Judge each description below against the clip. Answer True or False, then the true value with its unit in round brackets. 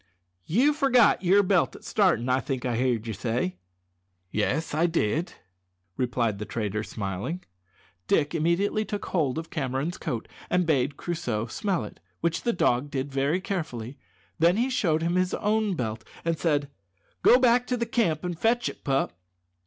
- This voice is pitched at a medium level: True (160 Hz)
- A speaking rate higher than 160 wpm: True (170 wpm)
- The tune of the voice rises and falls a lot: True (7.1 semitones)